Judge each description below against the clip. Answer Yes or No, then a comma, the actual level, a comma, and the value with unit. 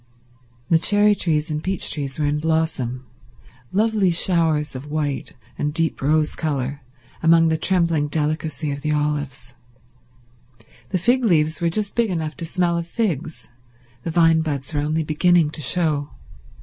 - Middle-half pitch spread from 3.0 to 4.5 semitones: No, narrow, 2.5 semitones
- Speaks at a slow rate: No, average, 150 wpm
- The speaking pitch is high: No, medium, 155 Hz